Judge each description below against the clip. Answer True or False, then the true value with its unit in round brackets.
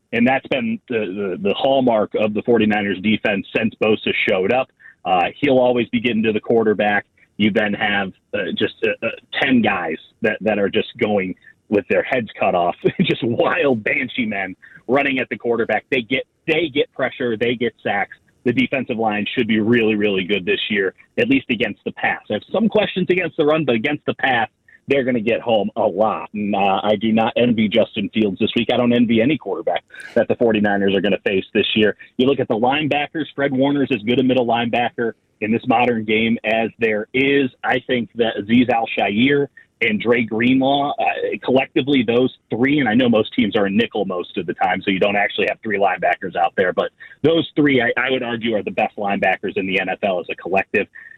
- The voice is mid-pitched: False (125 Hz)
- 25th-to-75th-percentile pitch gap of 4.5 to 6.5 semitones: True (4.9 semitones)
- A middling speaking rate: False (215 wpm)